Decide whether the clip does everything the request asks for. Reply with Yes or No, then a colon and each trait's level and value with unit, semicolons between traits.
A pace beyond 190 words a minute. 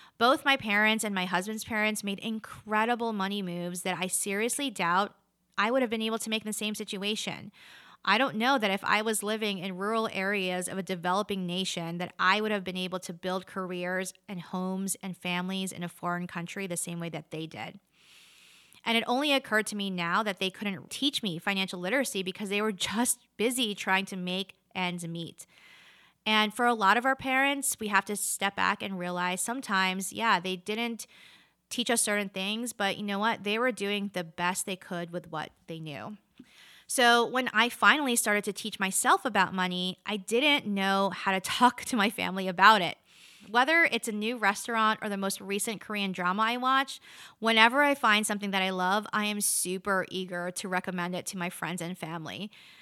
Yes: average, 200 wpm